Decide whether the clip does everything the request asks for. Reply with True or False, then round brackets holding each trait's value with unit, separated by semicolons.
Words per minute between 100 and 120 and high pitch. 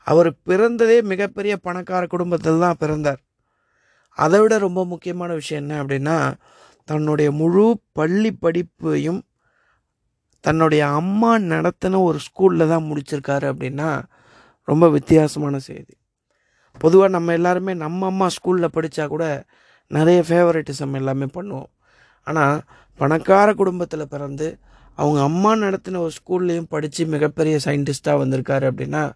False (115 wpm; 160 Hz)